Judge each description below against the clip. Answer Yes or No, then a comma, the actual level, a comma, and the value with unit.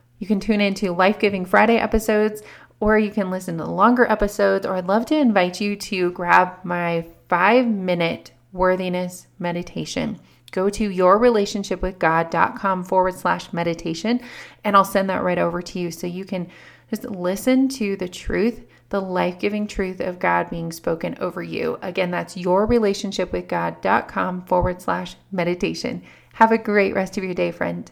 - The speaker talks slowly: No, average, 170 wpm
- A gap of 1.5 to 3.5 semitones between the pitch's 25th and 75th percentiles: Yes, average, 2.7 semitones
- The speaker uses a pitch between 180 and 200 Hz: Yes, medium, 185 Hz